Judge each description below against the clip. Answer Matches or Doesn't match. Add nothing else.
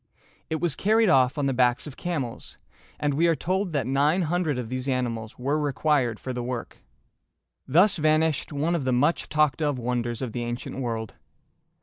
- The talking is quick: Doesn't match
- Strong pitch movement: Doesn't match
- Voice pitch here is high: Doesn't match